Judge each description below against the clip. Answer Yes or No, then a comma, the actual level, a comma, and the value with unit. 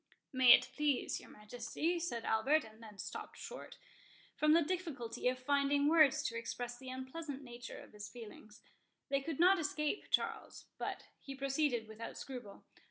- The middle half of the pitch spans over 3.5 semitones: Yes, average, 4.5 semitones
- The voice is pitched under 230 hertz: No, very high, 265 Hz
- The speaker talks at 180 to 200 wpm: No, average, 160 wpm